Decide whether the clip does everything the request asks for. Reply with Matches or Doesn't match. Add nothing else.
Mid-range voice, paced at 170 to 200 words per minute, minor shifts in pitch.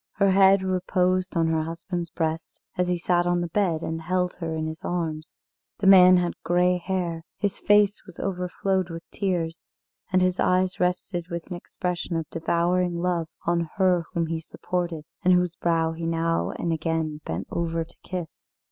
Matches